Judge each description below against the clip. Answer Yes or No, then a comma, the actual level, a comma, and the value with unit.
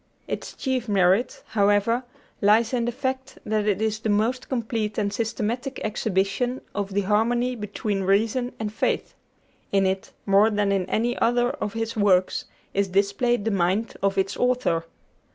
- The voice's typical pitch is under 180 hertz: No, high, 215 Hz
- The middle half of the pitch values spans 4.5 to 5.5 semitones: No, average, 3.3 semitones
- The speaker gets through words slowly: No, average, 160 wpm